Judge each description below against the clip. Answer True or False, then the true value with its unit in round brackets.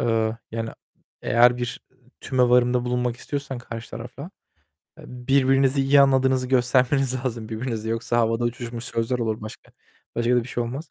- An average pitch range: False (2.0 semitones)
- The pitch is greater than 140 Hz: False (125 Hz)